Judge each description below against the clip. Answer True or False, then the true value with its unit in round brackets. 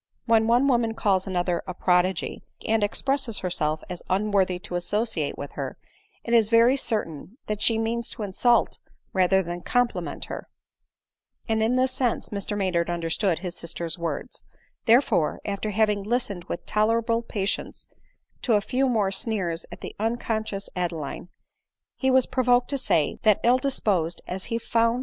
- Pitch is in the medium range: False (210 Hz)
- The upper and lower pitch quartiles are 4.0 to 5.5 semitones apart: True (4.5 semitones)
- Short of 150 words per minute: False (165 wpm)